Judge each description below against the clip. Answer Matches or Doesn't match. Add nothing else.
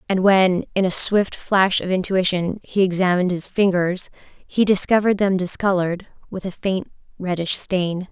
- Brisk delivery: Doesn't match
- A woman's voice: Matches